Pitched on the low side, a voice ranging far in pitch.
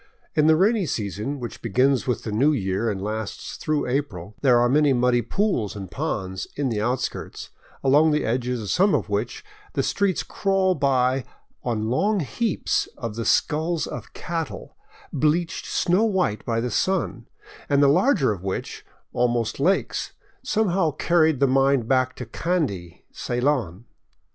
Yes: low, 130 Hz; wide, 5.7 semitones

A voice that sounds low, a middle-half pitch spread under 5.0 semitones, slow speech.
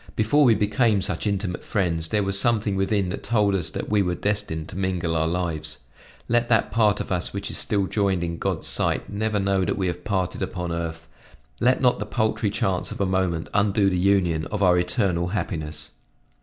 No: very low, 95 Hz; average, 3.0 semitones; fast, 205 wpm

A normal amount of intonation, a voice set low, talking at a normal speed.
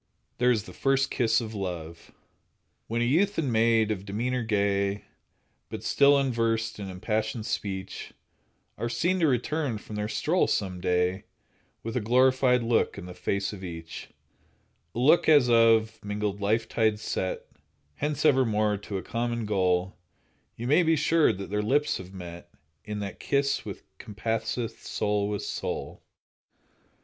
Yes: average, 3.8 semitones; low, 110 Hz; average, 155 wpm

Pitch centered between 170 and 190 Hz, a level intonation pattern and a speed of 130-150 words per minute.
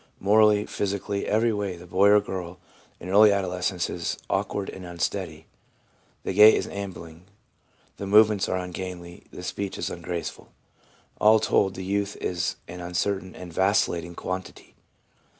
No: very low, 95 Hz; narrow, 2.3 semitones; average, 145 wpm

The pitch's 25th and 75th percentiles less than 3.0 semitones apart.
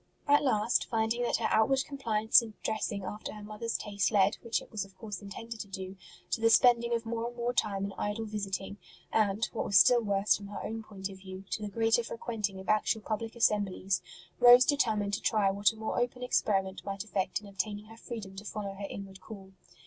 Yes: narrow, 2.5 semitones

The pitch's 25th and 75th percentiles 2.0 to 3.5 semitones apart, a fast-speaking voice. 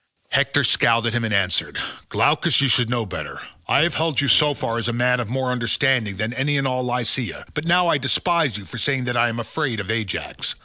Yes: average, 3.2 semitones; fast, 230 wpm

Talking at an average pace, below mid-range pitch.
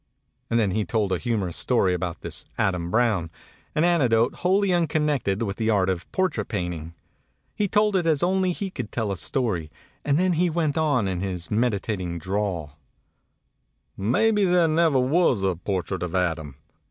Yes: average, 170 wpm; low, 110 Hz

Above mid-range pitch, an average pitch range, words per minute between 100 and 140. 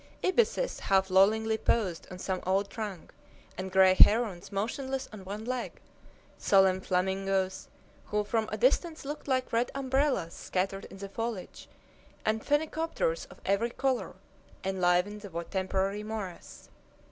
Yes: high, 205 Hz; average, 4.4 semitones; slow, 135 wpm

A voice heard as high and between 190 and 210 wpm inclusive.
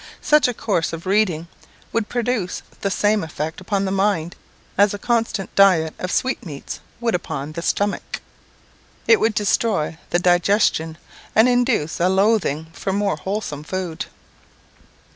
No: high, 195 Hz; average, 145 wpm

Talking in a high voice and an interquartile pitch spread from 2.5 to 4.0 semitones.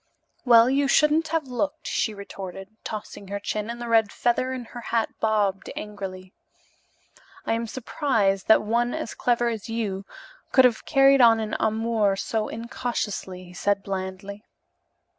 Yes: high, 225 Hz; average, 3.2 semitones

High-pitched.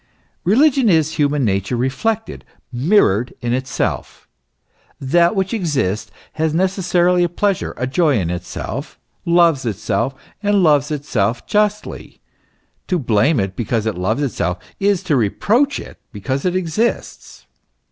No: medium, 150 Hz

